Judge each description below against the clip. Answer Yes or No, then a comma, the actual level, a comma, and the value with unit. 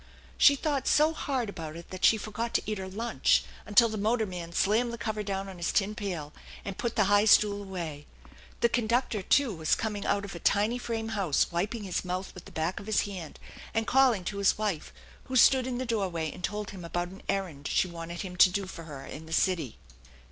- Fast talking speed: Yes, fast, 225 wpm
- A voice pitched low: No, high, 200 Hz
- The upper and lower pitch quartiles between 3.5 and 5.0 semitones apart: Yes, average, 4.1 semitones